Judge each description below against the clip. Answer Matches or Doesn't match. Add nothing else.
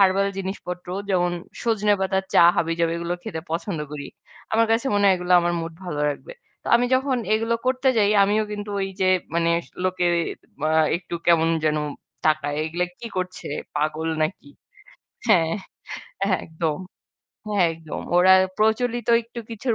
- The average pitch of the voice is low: Doesn't match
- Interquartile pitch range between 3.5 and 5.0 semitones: Matches